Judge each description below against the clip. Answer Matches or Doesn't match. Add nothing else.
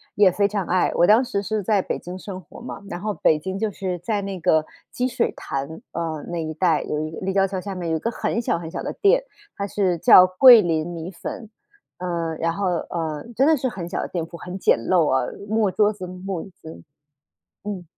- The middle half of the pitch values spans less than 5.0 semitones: Matches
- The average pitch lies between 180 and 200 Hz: Matches